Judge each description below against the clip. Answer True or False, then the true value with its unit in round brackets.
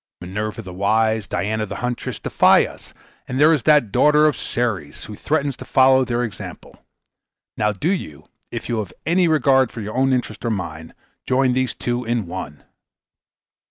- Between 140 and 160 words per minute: False (180 wpm)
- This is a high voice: False (120 Hz)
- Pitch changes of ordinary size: True (4.1 semitones)